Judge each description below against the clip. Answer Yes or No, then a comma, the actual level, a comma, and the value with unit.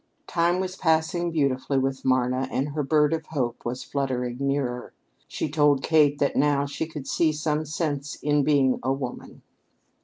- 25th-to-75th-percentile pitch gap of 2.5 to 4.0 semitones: Yes, average, 2.8 semitones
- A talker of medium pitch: Yes, medium, 145 Hz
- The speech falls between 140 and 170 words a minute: Yes, average, 165 wpm